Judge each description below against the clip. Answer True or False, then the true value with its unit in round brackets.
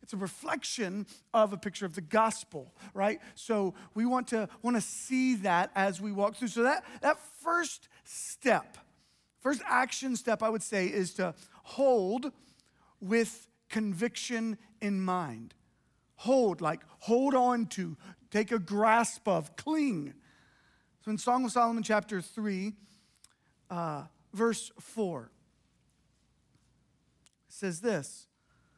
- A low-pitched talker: False (215 Hz)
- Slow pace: True (130 wpm)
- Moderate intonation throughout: True (3.9 semitones)